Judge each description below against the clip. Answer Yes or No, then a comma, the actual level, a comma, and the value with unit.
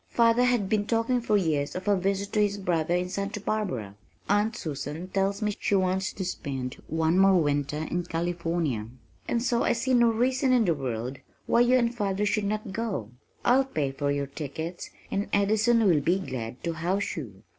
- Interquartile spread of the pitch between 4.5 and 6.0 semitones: Yes, wide, 5.5 semitones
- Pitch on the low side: No, high, 190 Hz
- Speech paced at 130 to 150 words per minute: No, average, 195 wpm